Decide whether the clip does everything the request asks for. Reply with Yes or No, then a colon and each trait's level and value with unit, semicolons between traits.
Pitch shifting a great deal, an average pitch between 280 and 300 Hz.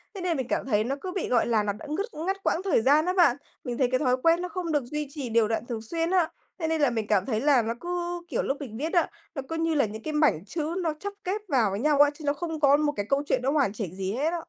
Yes: wide, 5.9 semitones; very high, 290 Hz